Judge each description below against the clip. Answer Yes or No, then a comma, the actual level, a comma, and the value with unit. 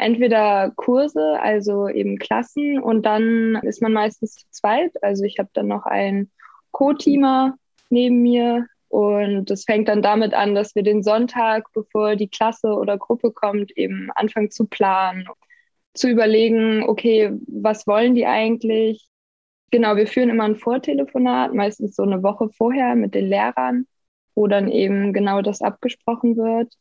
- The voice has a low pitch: No, high, 220 Hz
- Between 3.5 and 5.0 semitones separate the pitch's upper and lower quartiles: No, narrow, 2.6 semitones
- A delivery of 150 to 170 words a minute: Yes, average, 155 wpm